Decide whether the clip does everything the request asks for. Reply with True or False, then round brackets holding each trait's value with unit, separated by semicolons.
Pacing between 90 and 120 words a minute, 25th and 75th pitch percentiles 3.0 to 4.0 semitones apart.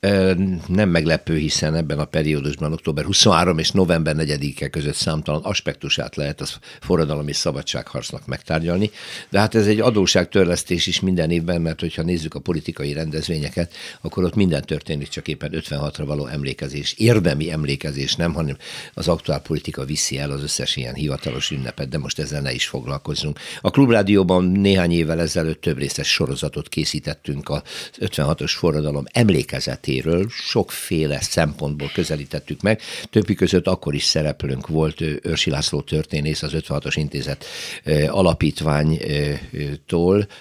False (140 wpm; 3.5 semitones)